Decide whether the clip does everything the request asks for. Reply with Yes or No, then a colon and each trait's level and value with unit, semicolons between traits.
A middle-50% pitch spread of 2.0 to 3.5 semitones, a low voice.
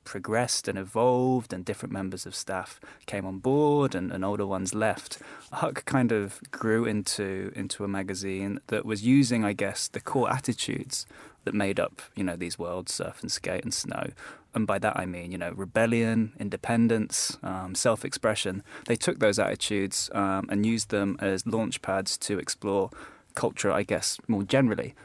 Yes: average, 2.9 semitones; low, 100 Hz